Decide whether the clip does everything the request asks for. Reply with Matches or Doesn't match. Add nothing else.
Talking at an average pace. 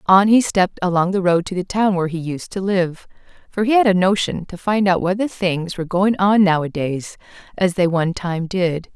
Doesn't match